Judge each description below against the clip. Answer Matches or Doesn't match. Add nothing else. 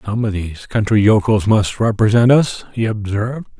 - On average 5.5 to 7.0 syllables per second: Doesn't match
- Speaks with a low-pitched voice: Matches